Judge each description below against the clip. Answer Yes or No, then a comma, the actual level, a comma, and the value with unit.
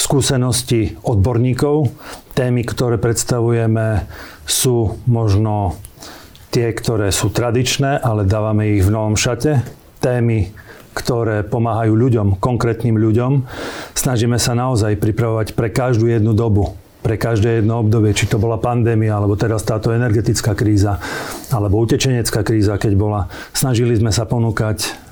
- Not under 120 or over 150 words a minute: Yes, average, 125 wpm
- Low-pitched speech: Yes, low, 115 Hz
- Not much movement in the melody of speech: Yes, narrow, 2.3 semitones